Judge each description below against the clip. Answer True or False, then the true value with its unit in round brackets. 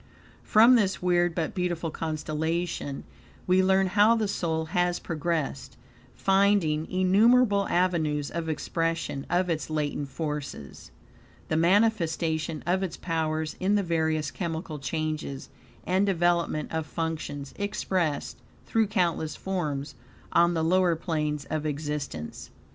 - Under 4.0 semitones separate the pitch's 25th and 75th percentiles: True (3.1 semitones)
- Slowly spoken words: True (120 wpm)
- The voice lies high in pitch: False (165 Hz)